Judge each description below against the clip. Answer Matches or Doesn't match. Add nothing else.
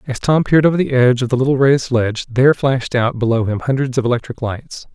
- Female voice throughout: Doesn't match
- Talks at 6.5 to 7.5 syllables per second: Matches